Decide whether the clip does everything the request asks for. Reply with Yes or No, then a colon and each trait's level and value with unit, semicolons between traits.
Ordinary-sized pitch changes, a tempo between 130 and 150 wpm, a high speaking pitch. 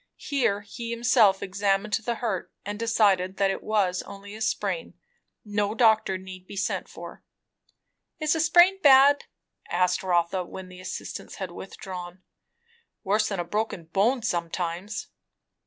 Yes: average, 3.5 semitones; average, 140 wpm; high, 200 Hz